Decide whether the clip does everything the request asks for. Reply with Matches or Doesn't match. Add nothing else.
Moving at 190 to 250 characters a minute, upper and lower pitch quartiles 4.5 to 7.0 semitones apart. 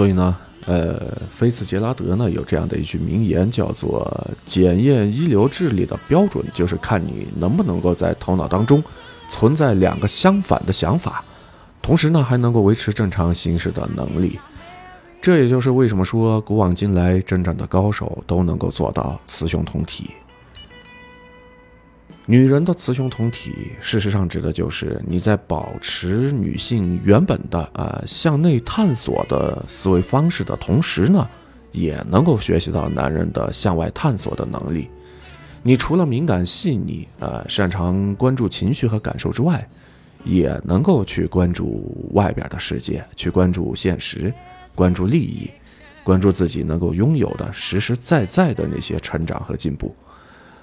Matches